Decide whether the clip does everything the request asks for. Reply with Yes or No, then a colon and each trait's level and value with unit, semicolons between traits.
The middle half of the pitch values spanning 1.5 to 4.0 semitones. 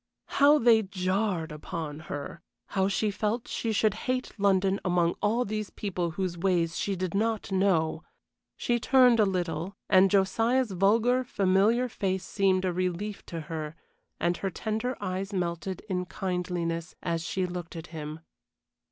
Yes: average, 3.5 semitones